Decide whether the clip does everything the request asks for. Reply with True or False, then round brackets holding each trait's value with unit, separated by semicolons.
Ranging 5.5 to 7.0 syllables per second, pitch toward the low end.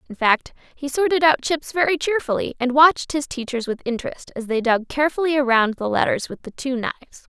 False (6.1 syllables/s; 270 Hz)